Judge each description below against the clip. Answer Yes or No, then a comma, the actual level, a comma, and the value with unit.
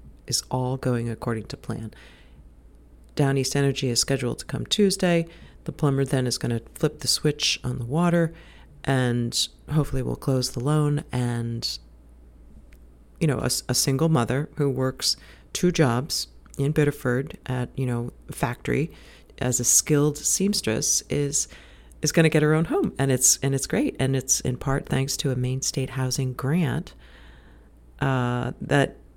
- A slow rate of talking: No, average, 165 wpm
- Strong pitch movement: No, average, 3.9 semitones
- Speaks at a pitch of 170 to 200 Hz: No, low, 130 Hz